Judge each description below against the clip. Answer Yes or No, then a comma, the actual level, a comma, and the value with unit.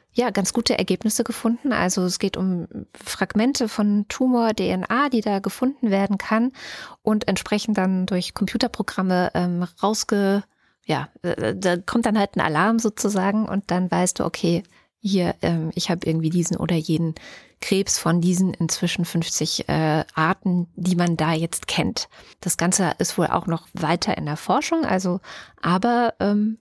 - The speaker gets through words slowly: No, average, 160 wpm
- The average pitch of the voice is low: No, high, 190 Hz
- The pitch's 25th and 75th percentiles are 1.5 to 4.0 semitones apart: Yes, average, 3.7 semitones